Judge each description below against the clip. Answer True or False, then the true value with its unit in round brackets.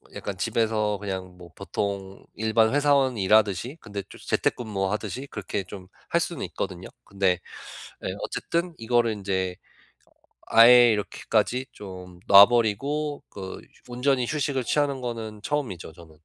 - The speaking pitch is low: True (110 Hz)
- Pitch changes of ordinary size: True (4.4 semitones)